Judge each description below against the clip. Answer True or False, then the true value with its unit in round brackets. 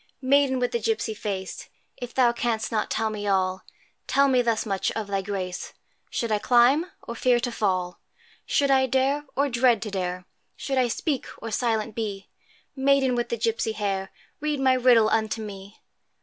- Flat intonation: False (3.8 semitones)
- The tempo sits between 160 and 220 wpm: True (180 wpm)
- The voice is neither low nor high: False (230 Hz)